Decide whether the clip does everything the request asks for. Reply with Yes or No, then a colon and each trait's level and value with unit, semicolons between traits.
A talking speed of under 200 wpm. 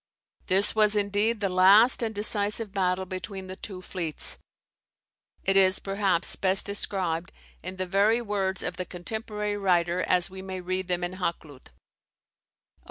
Yes: average, 160 wpm